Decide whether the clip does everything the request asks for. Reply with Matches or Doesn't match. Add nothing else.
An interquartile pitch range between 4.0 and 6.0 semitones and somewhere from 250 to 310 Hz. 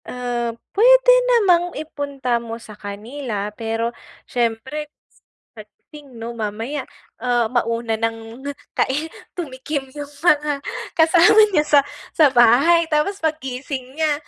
Matches